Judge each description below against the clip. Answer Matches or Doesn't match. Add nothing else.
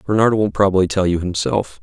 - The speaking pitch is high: Doesn't match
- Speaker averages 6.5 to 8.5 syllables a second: Doesn't match